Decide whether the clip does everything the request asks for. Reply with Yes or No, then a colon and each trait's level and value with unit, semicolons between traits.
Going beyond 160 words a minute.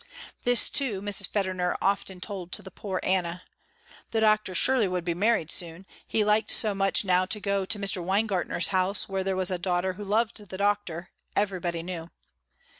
Yes: average, 180 wpm